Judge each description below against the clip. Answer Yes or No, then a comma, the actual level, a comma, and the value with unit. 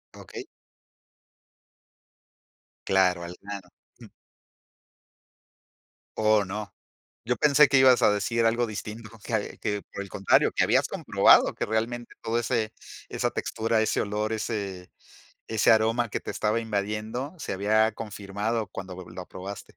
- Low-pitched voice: Yes, low, 110 Hz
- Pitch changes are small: Yes, narrow, 2.3 semitones